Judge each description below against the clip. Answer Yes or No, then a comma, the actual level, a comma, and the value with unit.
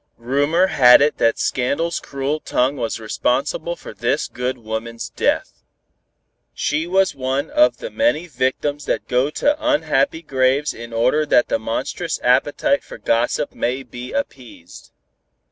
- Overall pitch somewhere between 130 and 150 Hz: Yes, low, 135 Hz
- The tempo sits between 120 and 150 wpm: Yes, average, 145 wpm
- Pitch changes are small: No, average, 4.4 semitones